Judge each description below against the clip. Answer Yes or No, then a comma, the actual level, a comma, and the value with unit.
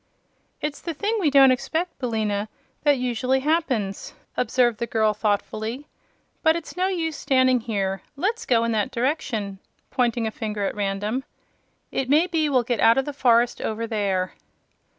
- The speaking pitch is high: Yes, high, 245 Hz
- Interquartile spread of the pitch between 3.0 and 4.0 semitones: No, average, 5.0 semitones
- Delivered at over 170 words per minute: No, average, 165 wpm